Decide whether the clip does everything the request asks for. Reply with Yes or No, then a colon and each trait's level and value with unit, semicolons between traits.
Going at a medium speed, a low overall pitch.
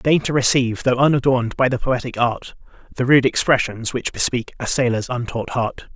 Yes: average, 180 wpm; low, 125 Hz